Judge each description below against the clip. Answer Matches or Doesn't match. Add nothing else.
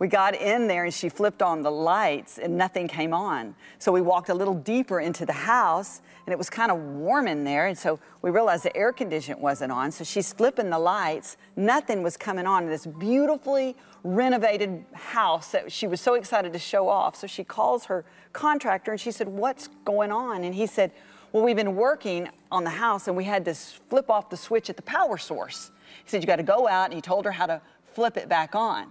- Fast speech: Matches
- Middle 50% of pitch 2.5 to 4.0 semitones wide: Doesn't match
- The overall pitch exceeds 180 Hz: Matches